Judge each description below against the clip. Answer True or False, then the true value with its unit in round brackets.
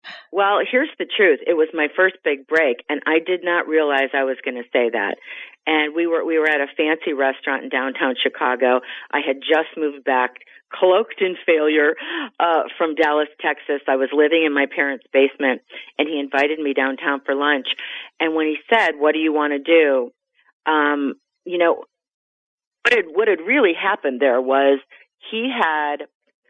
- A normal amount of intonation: True (3.4 semitones)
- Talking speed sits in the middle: True (190 wpm)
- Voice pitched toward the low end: False (150 Hz)